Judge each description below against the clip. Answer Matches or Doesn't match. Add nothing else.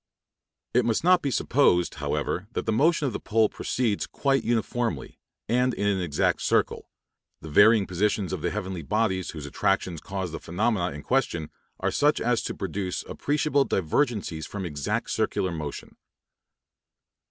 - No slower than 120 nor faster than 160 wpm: Matches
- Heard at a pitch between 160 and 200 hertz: Doesn't match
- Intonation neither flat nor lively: Doesn't match